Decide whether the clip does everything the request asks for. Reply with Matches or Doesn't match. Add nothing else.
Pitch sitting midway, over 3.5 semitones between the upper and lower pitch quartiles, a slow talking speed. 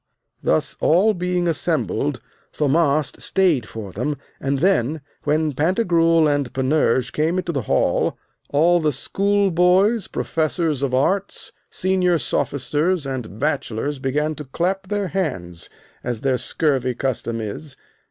Matches